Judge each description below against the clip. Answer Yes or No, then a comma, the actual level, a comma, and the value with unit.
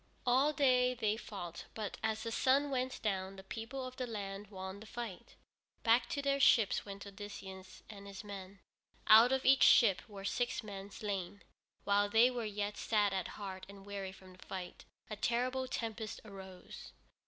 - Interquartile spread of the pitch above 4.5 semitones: No, average, 3.7 semitones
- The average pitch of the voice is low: No, high, 210 Hz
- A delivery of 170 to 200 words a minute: Yes, average, 175 wpm